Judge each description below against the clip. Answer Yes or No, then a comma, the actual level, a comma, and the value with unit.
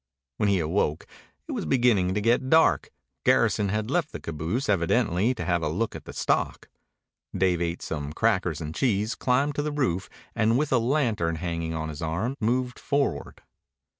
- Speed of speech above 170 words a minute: Yes, average, 180 wpm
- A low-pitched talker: Yes, low, 105 Hz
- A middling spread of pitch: No, wide, 7.0 semitones